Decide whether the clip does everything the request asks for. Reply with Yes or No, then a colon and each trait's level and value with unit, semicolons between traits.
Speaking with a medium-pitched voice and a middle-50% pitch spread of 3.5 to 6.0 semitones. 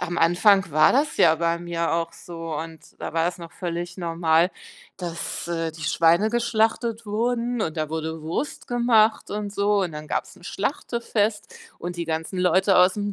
Yes: medium, 175 Hz; average, 4.1 semitones